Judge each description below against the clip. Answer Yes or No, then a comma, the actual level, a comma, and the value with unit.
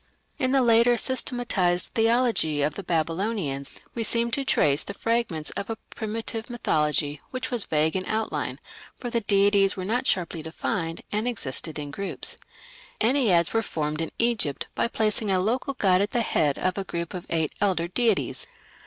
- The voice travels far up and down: Yes, wide, 6.0 semitones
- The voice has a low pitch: No, high, 200 Hz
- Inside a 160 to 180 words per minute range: Yes, average, 170 wpm